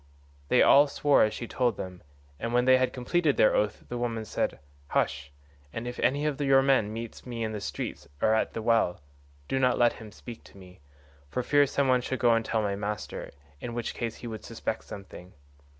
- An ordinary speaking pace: No, fast, 215 wpm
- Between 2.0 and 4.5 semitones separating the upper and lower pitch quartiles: Yes, average, 3.2 semitones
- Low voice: Yes, low, 115 Hz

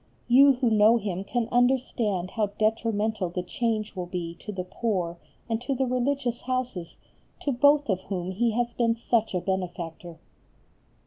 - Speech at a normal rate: Yes, average, 165 wpm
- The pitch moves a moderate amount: Yes, average, 4.7 semitones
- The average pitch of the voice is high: Yes, high, 220 Hz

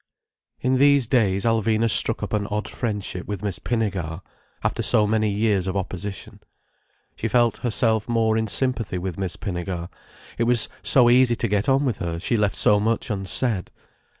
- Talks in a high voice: No, low, 110 Hz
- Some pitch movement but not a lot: Yes, average, 3.2 semitones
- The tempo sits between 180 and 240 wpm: No, average, 170 wpm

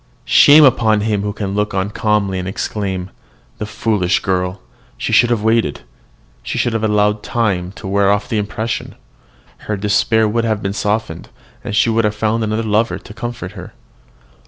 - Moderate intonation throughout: No, narrow, 2.1 semitones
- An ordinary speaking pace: Yes, average, 180 wpm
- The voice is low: Yes, low, 105 Hz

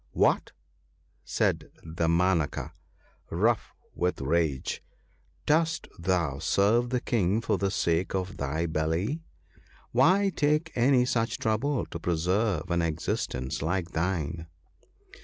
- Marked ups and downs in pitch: Yes, wide, 6.4 semitones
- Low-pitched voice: Yes, very low, 90 Hz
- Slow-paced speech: Yes, slow, 130 wpm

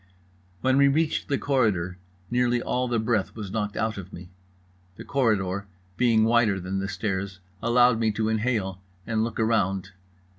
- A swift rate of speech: No, average, 160 wpm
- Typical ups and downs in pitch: Yes, average, 3.8 semitones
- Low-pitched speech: Yes, low, 110 Hz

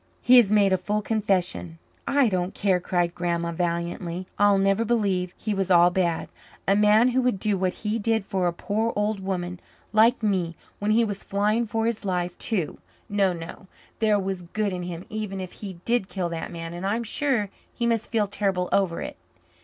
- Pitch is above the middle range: Yes, high, 195 Hz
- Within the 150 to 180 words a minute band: No, average, 200 wpm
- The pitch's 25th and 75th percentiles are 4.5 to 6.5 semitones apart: No, average, 3.2 semitones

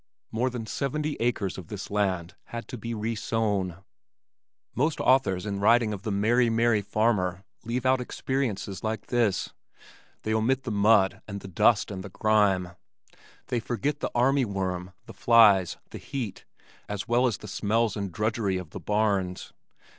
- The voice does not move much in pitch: No, average, 3.4 semitones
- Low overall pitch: Yes, low, 110 Hz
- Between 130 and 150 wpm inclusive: No, average, 160 wpm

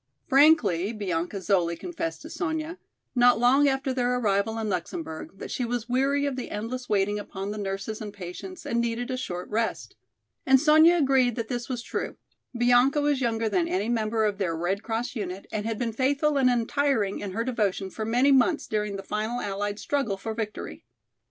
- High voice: Yes, high, 230 Hz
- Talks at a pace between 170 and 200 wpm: Yes, average, 190 wpm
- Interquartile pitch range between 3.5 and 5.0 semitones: Yes, average, 4.5 semitones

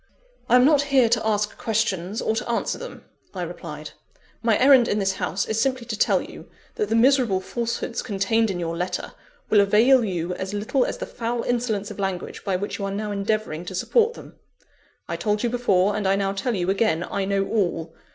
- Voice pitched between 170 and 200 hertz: No, high, 210 Hz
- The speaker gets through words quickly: Yes, fast, 210 wpm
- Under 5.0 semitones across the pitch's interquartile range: Yes, average, 3.5 semitones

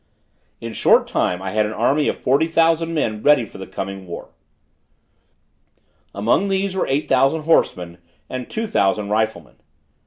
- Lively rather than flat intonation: Yes, wide, 8.1 semitones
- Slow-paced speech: No, average, 160 wpm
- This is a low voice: Yes, low, 120 Hz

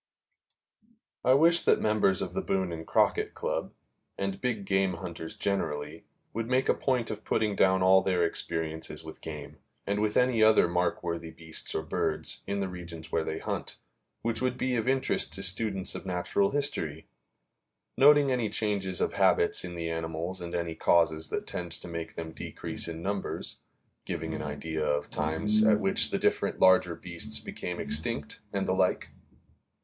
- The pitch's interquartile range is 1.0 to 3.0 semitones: No, average, 4.7 semitones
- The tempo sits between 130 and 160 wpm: No, average, 175 wpm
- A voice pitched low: Yes, very low, 90 Hz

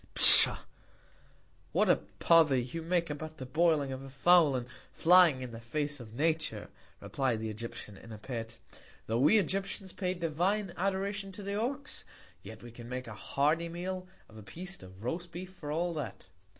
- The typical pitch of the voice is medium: Yes, medium, 155 Hz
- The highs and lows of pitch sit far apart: Yes, wide, 6.8 semitones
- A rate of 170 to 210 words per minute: Yes, average, 180 wpm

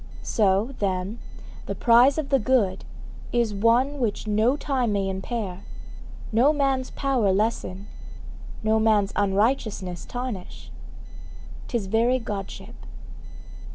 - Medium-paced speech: No, slow, 110 wpm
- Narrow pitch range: No, average, 4.3 semitones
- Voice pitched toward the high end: Yes, high, 220 Hz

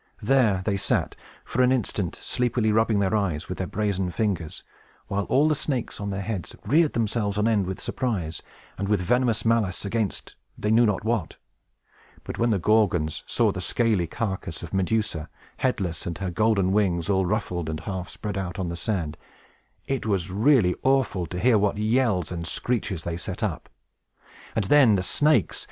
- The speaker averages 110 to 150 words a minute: No, average, 180 wpm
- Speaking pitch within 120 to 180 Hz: No, low, 100 Hz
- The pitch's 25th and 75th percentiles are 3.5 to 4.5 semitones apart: Yes, average, 3.9 semitones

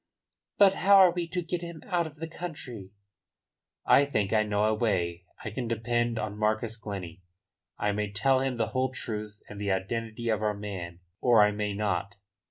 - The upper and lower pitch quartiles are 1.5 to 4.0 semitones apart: No, average, 4.4 semitones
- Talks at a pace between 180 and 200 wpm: Yes, average, 190 wpm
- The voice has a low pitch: Yes, low, 110 Hz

